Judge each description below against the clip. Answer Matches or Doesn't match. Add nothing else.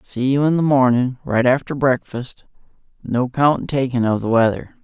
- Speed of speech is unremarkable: Matches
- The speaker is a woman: Doesn't match